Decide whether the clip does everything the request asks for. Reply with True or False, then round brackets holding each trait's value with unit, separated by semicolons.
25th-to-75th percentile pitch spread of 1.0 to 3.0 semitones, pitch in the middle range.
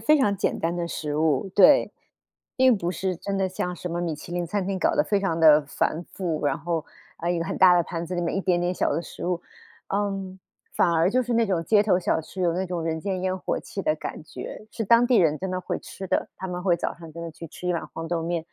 True (2.7 semitones; 180 Hz)